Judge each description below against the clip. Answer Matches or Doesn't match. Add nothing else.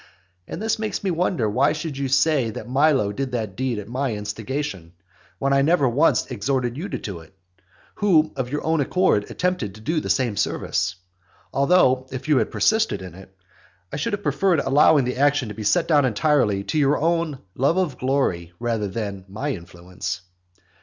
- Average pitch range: Doesn't match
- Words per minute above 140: Matches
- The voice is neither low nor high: Doesn't match